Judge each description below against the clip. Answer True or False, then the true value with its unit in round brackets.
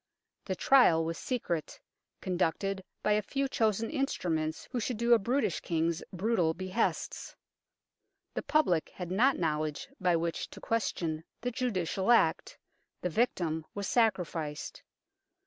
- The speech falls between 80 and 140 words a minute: True (135 wpm)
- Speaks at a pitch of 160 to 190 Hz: True (185 Hz)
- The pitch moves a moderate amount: False (5.9 semitones)